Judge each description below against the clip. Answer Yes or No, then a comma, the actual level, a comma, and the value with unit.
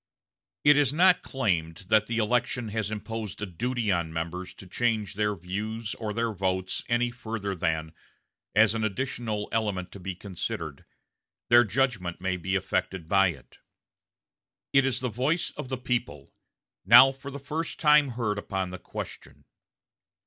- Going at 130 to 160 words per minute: Yes, average, 155 wpm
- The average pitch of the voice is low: Yes, low, 110 Hz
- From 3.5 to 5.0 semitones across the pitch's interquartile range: Yes, average, 4.6 semitones